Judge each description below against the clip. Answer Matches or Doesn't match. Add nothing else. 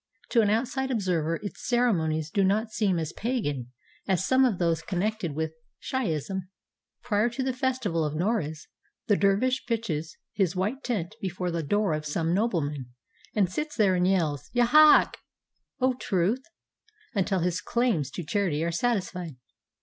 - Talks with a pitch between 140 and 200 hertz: Matches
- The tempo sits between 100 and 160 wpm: Matches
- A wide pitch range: Matches